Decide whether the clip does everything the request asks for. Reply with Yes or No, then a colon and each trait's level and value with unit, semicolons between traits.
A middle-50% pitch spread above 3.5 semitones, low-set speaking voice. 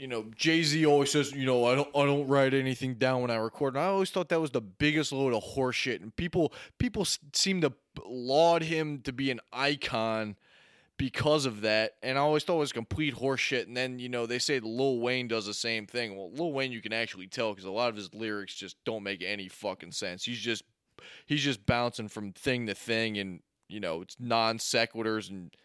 Yes: average, 4.2 semitones; low, 125 Hz